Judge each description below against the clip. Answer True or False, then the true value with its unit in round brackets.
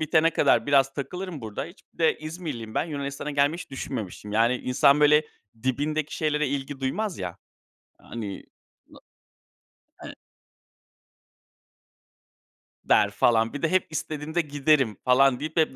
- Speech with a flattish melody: False (3.4 semitones)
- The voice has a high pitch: False (145 Hz)